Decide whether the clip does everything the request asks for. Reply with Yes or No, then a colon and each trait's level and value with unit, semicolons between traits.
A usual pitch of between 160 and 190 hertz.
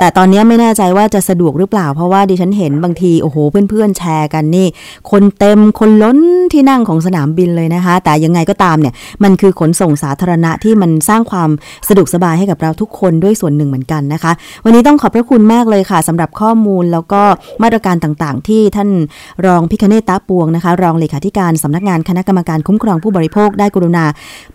Yes: medium, 185 Hz